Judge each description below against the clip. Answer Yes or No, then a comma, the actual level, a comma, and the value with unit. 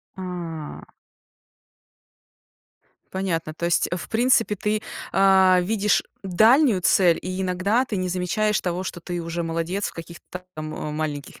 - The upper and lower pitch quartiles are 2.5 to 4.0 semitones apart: Yes, average, 3.0 semitones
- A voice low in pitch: No, medium, 185 Hz